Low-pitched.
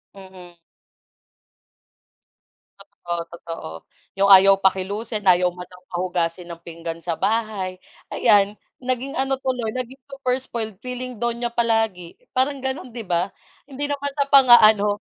No: high, 215 Hz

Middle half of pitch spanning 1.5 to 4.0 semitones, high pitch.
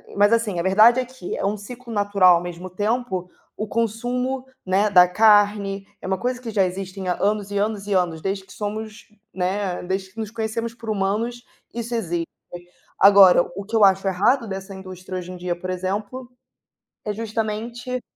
Yes: average, 3.1 semitones; high, 205 Hz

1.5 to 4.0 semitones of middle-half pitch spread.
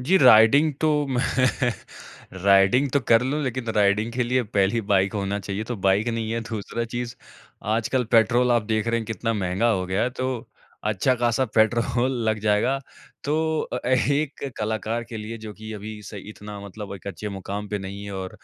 Yes: average, 3.4 semitones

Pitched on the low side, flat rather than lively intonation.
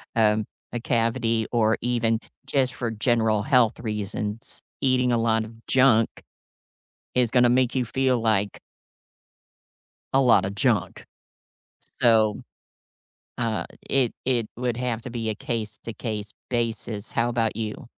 Yes: low, 115 Hz; narrow, 2.1 semitones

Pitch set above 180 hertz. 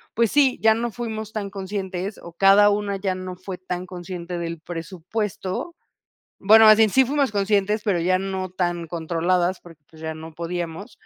Yes: high, 190 Hz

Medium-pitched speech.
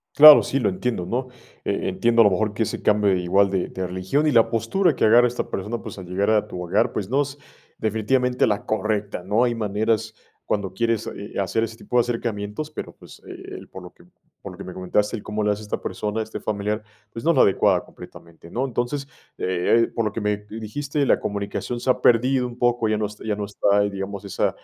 No: low, 110 Hz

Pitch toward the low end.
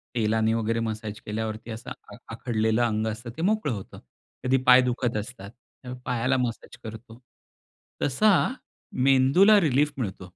Yes: low, 120 Hz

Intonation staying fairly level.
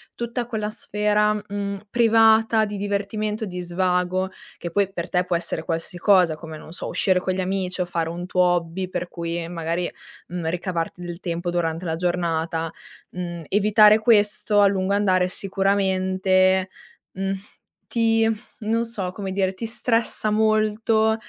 No: average, 3.1 semitones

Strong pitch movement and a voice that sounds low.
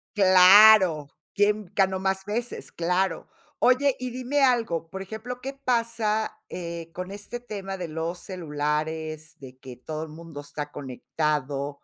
No: wide, 5.7 semitones; medium, 185 Hz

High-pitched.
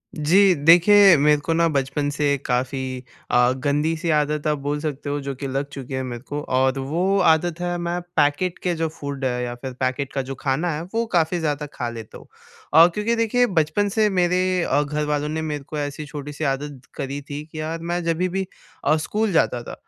No: medium, 150 Hz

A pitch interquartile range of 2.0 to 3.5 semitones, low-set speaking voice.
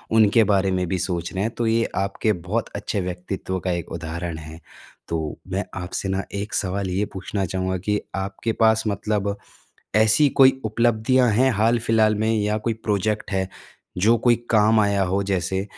Yes: average, 2.9 semitones; low, 100 Hz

